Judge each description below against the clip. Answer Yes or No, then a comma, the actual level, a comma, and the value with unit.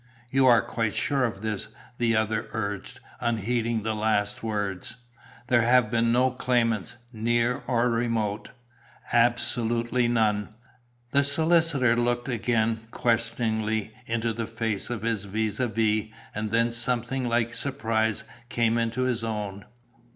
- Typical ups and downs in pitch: No, narrow, 1.7 semitones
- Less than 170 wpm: Yes, slow, 135 wpm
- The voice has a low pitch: Yes, low, 115 Hz